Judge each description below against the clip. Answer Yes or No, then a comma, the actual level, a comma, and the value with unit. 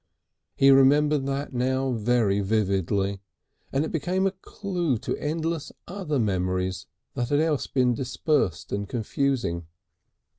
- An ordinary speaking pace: No, slow, 125 wpm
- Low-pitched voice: Yes, low, 130 Hz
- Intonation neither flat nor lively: No, wide, 6.7 semitones